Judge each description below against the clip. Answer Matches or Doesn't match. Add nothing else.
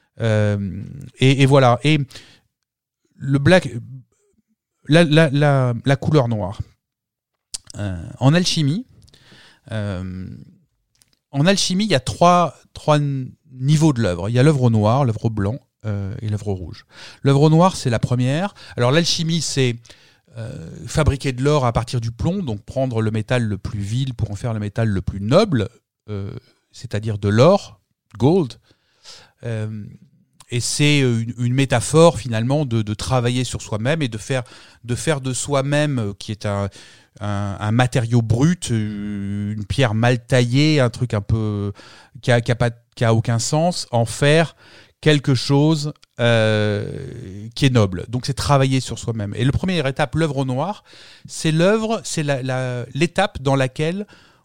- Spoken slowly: Doesn't match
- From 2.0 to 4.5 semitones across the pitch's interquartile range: Doesn't match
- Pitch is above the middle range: Doesn't match